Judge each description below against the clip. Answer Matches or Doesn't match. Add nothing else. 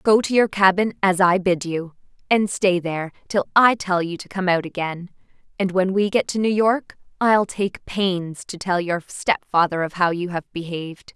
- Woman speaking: Matches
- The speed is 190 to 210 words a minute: Matches